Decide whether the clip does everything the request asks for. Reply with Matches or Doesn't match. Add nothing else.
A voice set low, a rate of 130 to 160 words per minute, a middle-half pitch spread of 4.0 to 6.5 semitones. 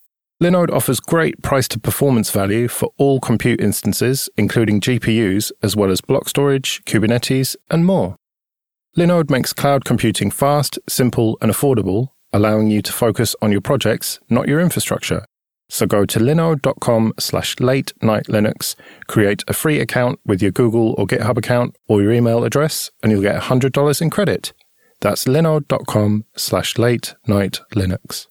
Matches